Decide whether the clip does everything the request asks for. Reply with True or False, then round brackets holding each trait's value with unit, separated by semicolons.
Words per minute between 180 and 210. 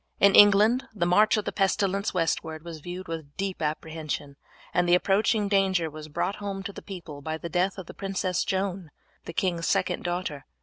True (190 wpm)